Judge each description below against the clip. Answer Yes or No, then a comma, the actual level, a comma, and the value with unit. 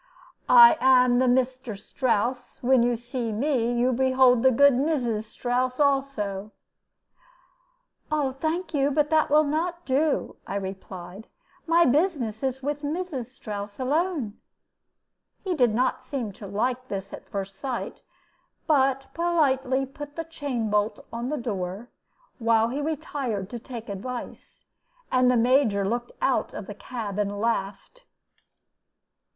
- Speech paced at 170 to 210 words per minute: No, slow, 135 wpm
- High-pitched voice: Yes, very high, 255 Hz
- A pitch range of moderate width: Yes, average, 4.2 semitones